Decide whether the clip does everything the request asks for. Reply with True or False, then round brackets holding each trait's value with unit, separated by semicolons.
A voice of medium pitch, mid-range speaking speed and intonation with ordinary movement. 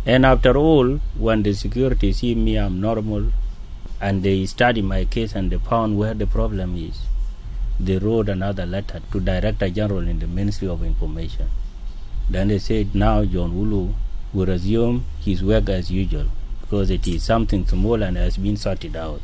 False (100 Hz; 175 wpm; 3.1 semitones)